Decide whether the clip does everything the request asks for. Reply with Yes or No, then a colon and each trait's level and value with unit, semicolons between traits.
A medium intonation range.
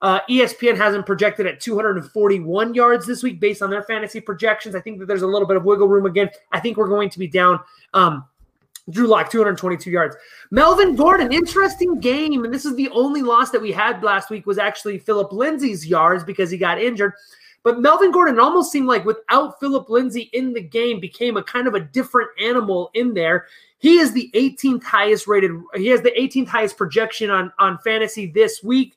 Yes: average, 4.0 semitones